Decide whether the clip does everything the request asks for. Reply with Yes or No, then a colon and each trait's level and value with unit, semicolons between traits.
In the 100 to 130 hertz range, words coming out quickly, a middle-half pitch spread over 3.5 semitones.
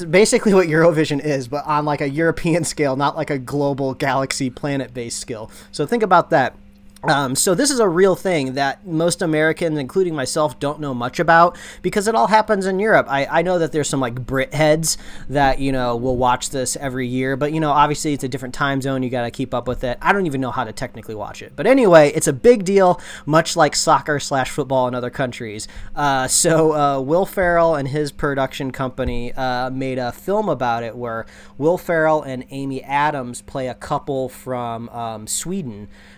No: medium, 140 Hz; fast, 210 wpm; average, 4.0 semitones